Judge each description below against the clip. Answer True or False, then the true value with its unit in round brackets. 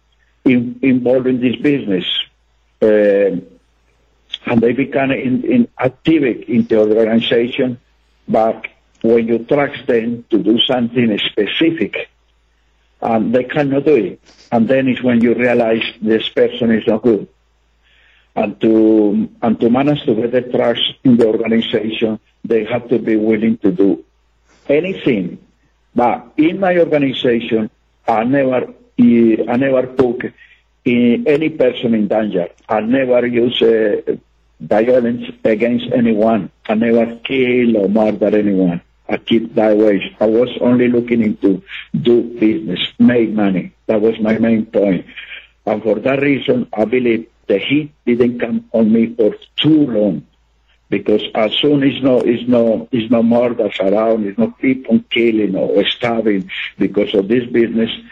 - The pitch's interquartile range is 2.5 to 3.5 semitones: True (2.8 semitones)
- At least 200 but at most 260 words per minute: False (145 wpm)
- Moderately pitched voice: False (115 Hz)